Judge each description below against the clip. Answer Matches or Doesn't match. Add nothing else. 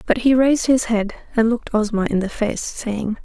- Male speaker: Doesn't match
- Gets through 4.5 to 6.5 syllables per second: Matches